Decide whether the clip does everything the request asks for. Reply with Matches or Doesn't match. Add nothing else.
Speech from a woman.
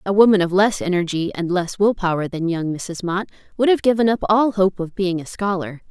Matches